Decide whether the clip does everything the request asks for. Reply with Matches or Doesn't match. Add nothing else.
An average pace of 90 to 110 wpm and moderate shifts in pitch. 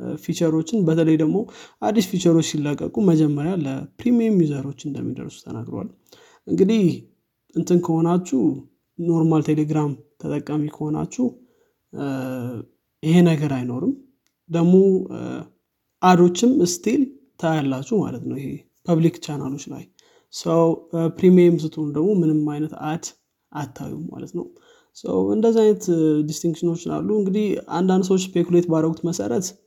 Matches